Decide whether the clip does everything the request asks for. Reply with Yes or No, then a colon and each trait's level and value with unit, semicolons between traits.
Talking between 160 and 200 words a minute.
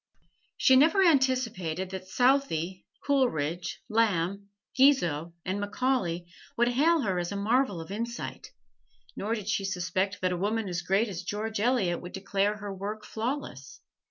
No: average, 150 wpm